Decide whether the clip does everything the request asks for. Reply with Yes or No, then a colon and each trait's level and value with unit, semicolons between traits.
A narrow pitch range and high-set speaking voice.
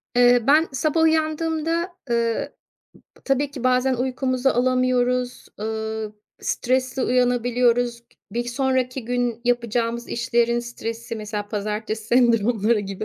Yes: narrow, 1.9 semitones; high, 245 Hz